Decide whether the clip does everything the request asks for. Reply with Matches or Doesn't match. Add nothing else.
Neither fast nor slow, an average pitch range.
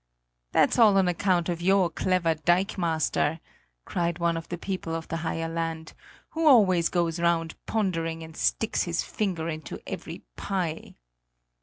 Doesn't match